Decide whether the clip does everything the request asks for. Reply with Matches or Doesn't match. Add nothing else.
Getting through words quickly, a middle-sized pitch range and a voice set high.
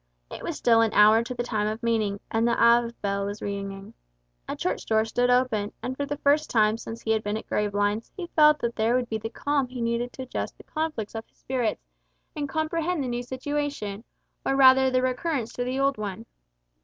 Matches